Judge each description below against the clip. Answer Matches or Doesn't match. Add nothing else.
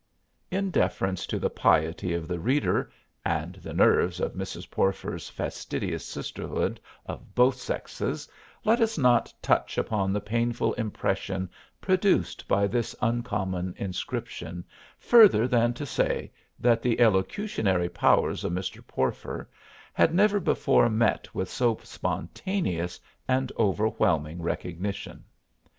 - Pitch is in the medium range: Doesn't match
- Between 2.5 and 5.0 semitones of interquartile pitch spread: Doesn't match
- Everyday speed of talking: Doesn't match